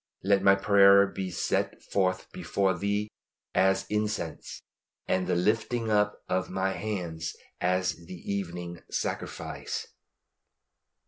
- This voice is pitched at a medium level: No, very low, 95 Hz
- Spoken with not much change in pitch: Yes, narrow, 1.8 semitones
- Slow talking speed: Yes, slow, 115 wpm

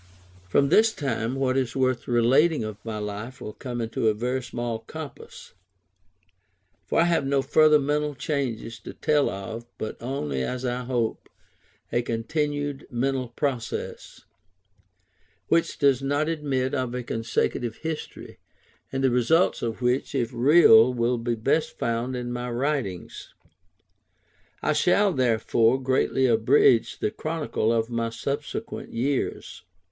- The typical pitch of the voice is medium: No, low, 125 Hz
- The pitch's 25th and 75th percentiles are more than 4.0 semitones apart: No, average, 3.5 semitones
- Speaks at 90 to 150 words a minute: Yes, average, 140 wpm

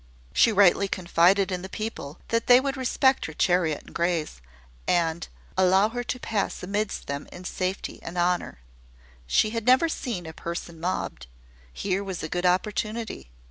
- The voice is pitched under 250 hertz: Yes, medium, 185 Hz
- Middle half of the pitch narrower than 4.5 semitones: Yes, average, 4.0 semitones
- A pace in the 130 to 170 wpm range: Yes, average, 165 wpm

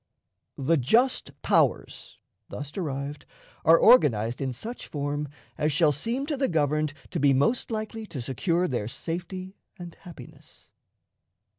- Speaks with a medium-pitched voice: Yes, medium, 155 Hz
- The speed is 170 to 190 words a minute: No, slow, 135 wpm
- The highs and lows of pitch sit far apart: Yes, wide, 5.7 semitones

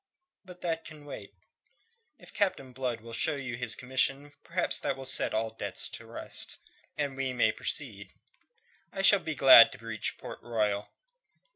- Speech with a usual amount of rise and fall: Yes, average, 4.2 semitones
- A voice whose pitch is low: Yes, low, 130 Hz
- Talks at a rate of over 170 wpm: No, average, 165 wpm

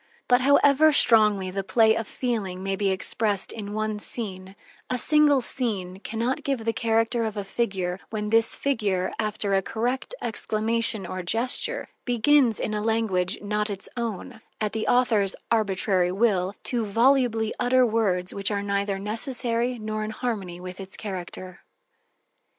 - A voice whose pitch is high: Yes, high, 215 Hz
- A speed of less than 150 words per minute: No, average, 155 wpm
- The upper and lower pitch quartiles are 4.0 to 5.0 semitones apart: No, average, 3.3 semitones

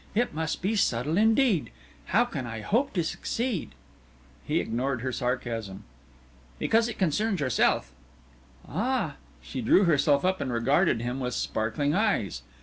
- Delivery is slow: No, average, 145 wpm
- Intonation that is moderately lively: No, wide, 9.0 semitones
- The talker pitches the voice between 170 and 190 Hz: No, medium, 150 Hz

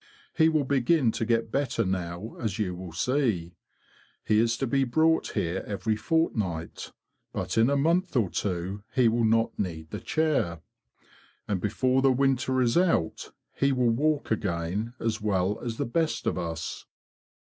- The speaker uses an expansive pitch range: Yes, wide, 6.1 semitones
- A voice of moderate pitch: No, low, 115 Hz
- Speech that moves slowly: No, average, 165 wpm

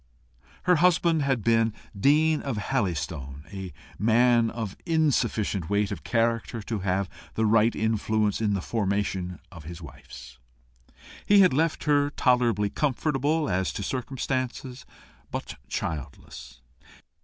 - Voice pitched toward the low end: Yes, low, 115 Hz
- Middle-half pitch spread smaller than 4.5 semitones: No, wide, 5.6 semitones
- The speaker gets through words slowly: Yes, slow, 125 wpm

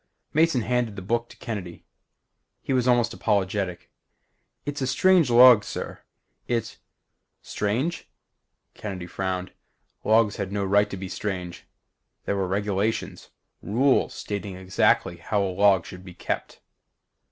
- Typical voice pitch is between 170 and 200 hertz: No, low, 105 Hz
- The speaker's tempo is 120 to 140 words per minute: Yes, slow, 135 wpm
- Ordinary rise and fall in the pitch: Yes, average, 4.1 semitones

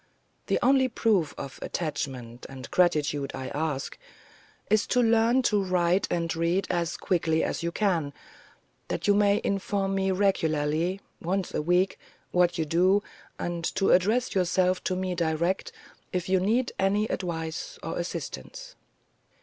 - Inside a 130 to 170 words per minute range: Yes, average, 145 wpm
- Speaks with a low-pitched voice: No, medium, 180 Hz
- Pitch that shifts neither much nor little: Yes, average, 3.6 semitones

